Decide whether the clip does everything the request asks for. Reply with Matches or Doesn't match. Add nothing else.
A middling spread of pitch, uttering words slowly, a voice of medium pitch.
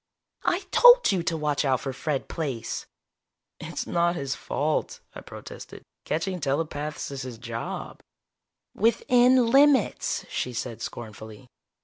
Doesn't match